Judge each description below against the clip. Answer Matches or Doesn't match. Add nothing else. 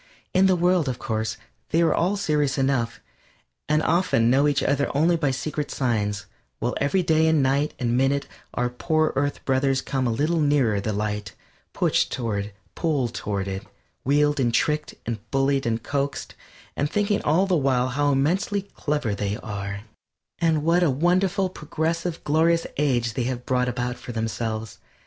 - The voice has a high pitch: Doesn't match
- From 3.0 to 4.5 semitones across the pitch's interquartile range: Doesn't match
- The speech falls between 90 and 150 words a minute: Doesn't match